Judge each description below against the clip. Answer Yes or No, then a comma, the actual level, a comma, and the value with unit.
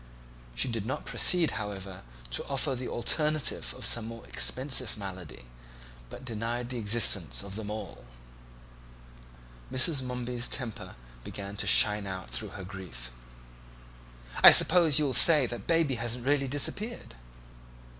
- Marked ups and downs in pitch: No, average, 4.9 semitones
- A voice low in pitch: Yes, low, 120 Hz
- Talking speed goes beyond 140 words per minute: No, slow, 135 wpm